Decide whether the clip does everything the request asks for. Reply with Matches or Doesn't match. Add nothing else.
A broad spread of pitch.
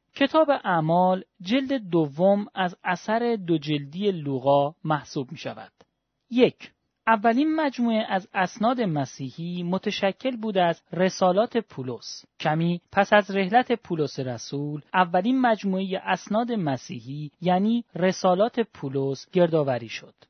Matches